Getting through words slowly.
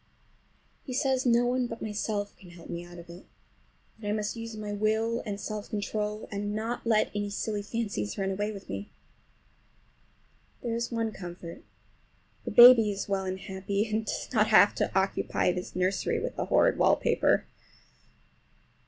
No: average, 165 wpm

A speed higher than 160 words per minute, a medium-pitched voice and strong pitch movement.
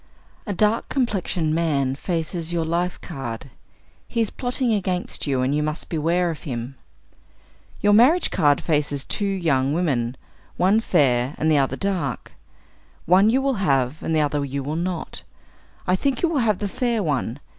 Yes: average, 170 wpm; medium, 165 Hz; wide, 5.9 semitones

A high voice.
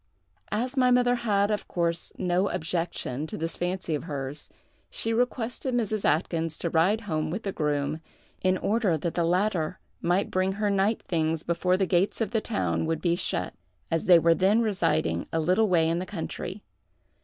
No: medium, 180 Hz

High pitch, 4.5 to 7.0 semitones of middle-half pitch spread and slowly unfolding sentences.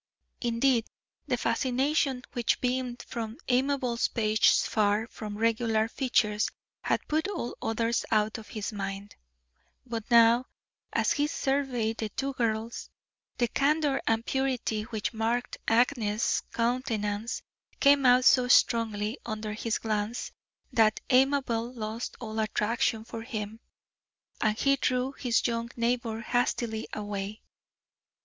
No: high, 230 Hz; narrow, 2.5 semitones; slow, 125 wpm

